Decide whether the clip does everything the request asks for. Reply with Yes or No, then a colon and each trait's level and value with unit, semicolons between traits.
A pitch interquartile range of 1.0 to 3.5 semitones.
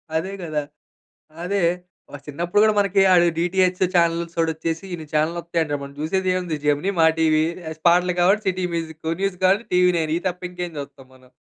Yes: narrow, 2.5 semitones